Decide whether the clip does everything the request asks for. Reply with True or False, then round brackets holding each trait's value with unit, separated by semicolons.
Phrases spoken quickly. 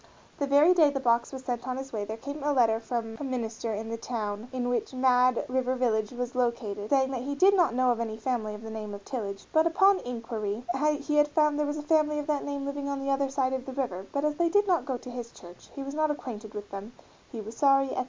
True (270 wpm)